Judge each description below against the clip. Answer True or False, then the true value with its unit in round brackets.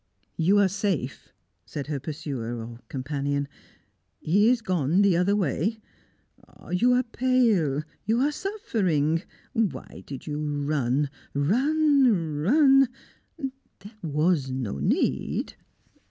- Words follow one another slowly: True (115 wpm)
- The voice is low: False (175 Hz)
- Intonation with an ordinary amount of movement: False (8.3 semitones)